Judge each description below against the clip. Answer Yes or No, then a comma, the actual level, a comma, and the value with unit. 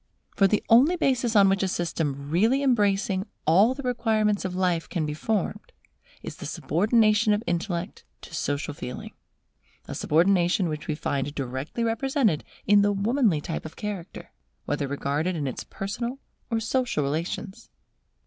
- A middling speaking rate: Yes, average, 155 wpm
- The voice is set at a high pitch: Yes, high, 195 Hz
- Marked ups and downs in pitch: Yes, wide, 5.9 semitones